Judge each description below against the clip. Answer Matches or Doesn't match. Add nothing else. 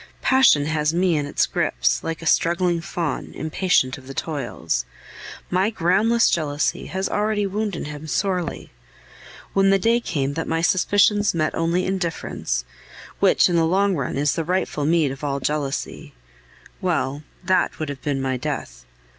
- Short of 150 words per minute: Doesn't match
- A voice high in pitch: Doesn't match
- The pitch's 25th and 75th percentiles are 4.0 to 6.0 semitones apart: Matches